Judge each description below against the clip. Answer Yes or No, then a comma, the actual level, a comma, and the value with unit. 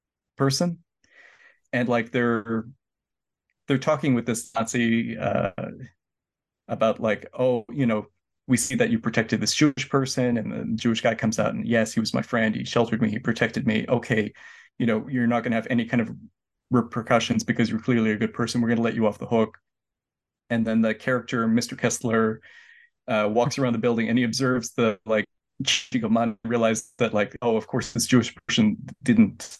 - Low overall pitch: Yes, low, 115 Hz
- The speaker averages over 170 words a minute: Yes, average, 190 wpm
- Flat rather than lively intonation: Yes, narrow, 2.1 semitones